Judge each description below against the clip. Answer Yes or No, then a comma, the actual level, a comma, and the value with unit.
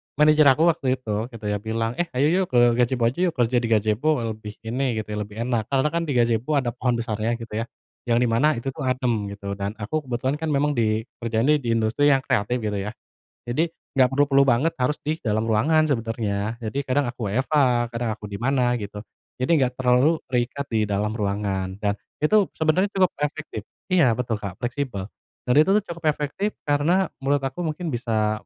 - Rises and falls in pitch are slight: No, average, 4.7 semitones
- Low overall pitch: Yes, low, 125 Hz